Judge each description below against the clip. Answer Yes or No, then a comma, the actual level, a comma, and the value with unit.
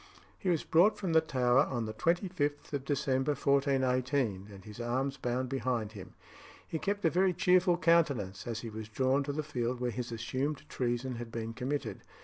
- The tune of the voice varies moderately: Yes, average, 4.1 semitones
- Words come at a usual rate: Yes, average, 185 wpm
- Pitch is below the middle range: Yes, low, 130 Hz